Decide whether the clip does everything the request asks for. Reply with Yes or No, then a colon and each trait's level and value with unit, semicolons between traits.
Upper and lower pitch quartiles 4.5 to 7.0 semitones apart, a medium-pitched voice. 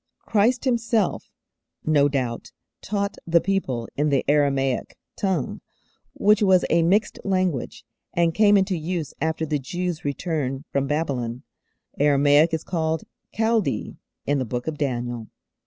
Yes: wide, 5.4 semitones; medium, 160 Hz